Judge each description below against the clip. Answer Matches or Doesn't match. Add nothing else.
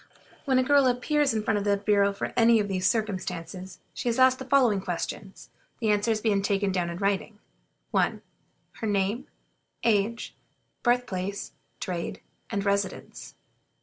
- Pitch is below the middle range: Doesn't match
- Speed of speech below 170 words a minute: Matches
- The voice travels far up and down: Doesn't match